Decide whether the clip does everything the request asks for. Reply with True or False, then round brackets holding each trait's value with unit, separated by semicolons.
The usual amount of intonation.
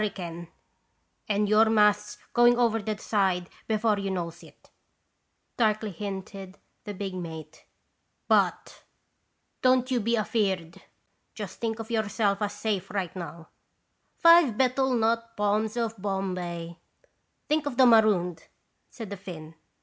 True (3.3 semitones)